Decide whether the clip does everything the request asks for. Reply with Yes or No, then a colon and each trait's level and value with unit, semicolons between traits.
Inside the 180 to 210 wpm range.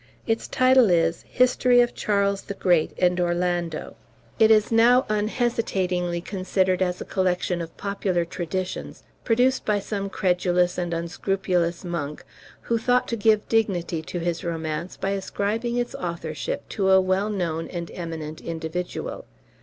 No: average, 145 wpm